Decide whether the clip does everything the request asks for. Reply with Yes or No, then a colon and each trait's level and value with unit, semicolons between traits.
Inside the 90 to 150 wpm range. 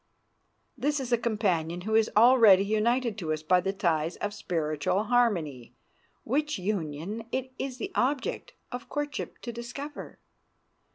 Yes: average, 140 wpm